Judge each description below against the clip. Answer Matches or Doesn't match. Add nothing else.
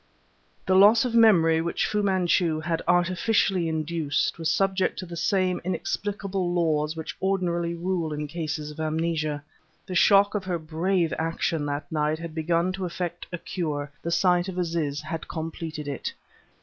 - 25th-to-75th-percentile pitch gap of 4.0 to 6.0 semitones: Doesn't match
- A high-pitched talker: Doesn't match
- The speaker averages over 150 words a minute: Matches